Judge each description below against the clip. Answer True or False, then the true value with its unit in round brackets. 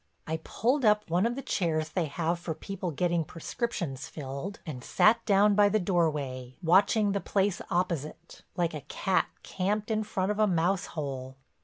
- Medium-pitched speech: True (180 Hz)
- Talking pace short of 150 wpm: False (175 wpm)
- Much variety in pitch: False (4.5 semitones)